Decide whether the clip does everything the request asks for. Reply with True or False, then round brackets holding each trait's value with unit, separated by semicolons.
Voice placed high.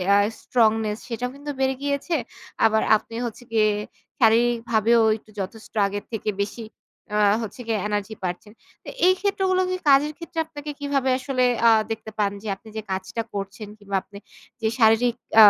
True (225 Hz)